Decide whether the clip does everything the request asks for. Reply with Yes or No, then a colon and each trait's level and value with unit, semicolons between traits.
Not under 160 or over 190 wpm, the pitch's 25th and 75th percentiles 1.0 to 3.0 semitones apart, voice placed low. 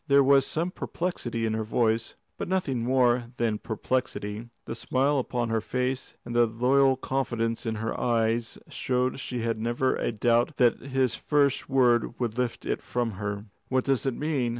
Yes: average, 175 wpm; narrow, 2.5 semitones; low, 120 Hz